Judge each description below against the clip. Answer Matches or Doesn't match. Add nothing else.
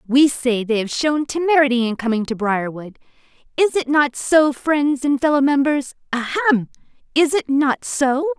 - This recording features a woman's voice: Matches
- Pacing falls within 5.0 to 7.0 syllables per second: Doesn't match